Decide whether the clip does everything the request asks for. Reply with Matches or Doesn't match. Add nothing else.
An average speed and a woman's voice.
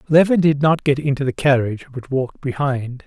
Doesn't match